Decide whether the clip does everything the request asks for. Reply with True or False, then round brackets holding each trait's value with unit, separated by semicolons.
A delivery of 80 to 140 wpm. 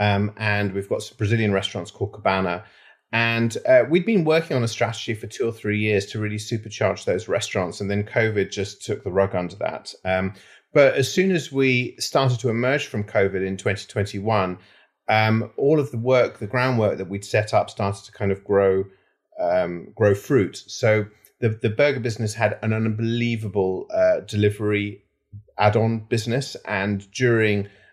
False (175 wpm)